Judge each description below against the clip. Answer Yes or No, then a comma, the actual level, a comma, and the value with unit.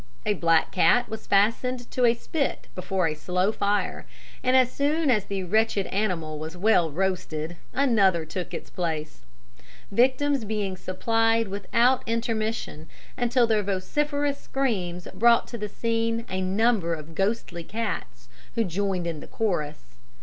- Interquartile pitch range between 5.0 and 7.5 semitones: No, average, 4.6 semitones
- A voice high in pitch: Yes, high, 205 Hz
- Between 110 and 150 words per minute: Yes, average, 145 wpm